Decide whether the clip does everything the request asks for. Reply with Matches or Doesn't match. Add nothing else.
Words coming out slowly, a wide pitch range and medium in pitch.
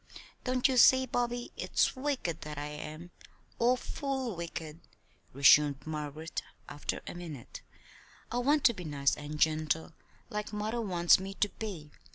Doesn't match